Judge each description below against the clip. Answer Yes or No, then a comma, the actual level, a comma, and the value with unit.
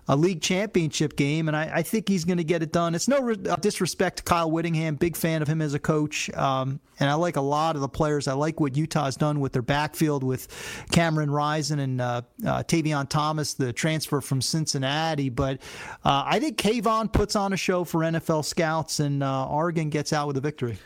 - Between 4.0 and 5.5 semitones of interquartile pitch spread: No, average, 3.2 semitones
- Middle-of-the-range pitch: Yes, medium, 155 Hz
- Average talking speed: No, fast, 220 wpm